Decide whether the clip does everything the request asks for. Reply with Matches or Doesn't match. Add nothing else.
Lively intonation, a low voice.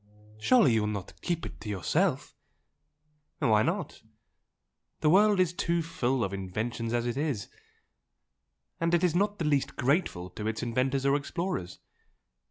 Matches